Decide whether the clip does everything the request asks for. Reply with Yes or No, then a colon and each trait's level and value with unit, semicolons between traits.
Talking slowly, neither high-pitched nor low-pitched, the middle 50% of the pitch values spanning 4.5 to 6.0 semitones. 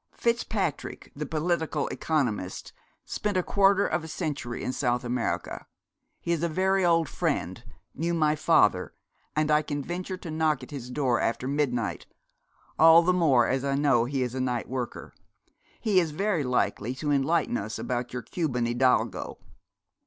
No: average, 165 wpm; medium, 150 Hz; average, 5.1 semitones